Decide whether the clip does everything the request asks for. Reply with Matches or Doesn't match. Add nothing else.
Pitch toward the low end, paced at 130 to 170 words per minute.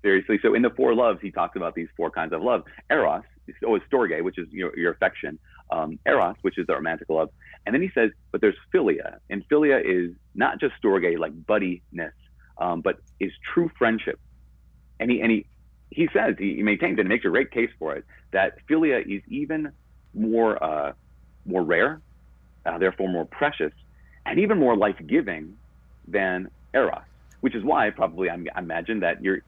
Doesn't match